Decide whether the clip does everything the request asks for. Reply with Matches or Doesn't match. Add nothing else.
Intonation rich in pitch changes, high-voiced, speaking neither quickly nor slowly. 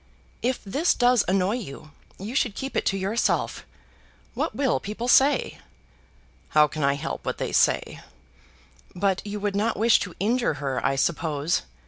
Matches